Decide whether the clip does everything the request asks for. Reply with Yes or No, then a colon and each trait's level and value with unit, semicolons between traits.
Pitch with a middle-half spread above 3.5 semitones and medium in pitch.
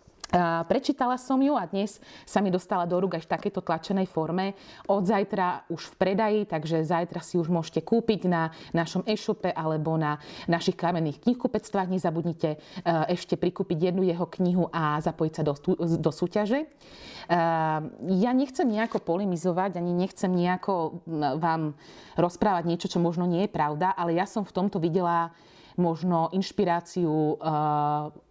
No: average, 2.8 semitones; medium, 175 Hz